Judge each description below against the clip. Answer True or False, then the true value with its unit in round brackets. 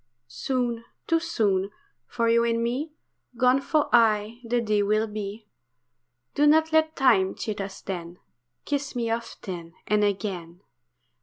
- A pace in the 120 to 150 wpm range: True (140 wpm)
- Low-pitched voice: False (230 Hz)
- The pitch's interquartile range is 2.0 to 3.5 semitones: False (4.0 semitones)